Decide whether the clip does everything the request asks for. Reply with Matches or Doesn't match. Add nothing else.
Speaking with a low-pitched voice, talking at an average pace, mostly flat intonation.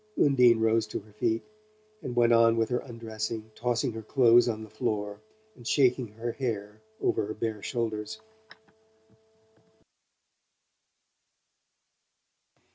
Doesn't match